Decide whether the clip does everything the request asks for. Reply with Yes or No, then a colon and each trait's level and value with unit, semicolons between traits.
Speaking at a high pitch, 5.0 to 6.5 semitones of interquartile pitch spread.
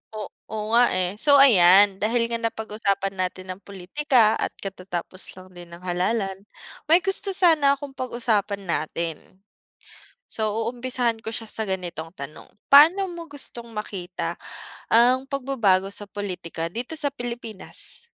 Yes: high, 220 Hz; wide, 5.4 semitones